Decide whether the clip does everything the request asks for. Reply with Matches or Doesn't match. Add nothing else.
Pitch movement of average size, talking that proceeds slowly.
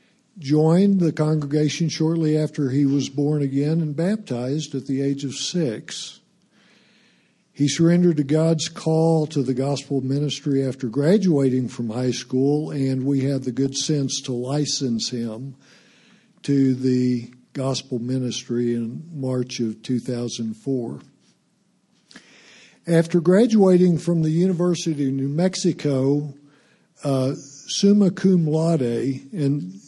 Matches